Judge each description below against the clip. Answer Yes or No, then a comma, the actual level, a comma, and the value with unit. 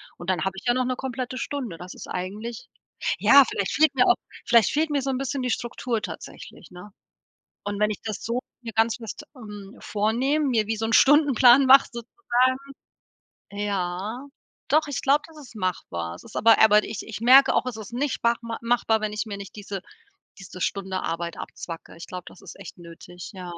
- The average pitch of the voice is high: Yes, high, 225 Hz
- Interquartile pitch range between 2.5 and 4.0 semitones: No, average, 4.5 semitones